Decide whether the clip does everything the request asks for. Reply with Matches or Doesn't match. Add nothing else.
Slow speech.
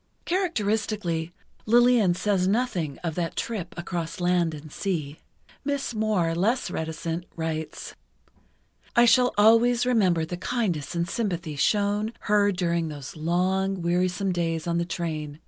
Matches